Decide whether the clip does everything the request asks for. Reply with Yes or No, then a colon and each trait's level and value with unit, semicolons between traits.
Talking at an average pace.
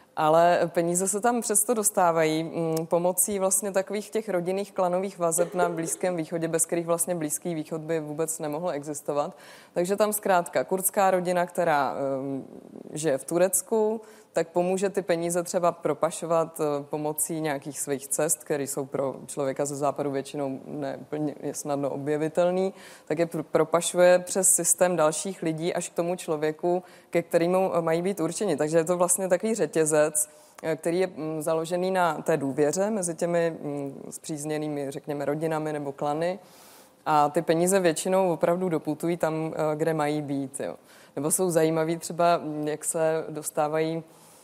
Yes: average, 145 wpm